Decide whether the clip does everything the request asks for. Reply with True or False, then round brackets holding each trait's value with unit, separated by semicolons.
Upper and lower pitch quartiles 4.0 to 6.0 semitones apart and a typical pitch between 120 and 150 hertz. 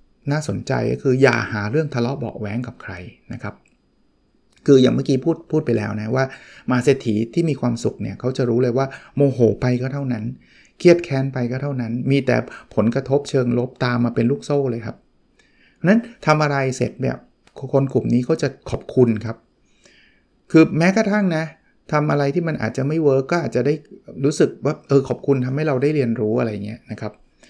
False (3.3 semitones; 130 Hz)